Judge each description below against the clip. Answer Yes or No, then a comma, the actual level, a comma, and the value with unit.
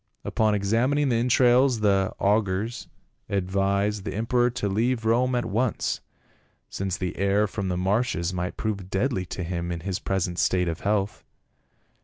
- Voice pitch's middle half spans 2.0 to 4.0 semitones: Yes, average, 3.7 semitones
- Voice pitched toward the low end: Yes, low, 100 Hz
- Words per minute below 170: Yes, average, 160 wpm